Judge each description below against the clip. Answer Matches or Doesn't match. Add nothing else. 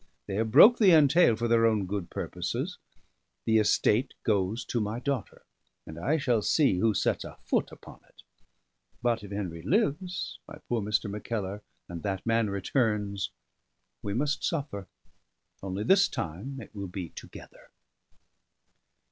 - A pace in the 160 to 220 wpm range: Doesn't match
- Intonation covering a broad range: Doesn't match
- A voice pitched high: Doesn't match